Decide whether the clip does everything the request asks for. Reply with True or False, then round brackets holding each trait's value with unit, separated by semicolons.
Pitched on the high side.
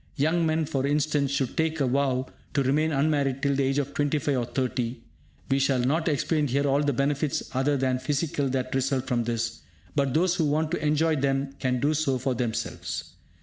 False (140 Hz)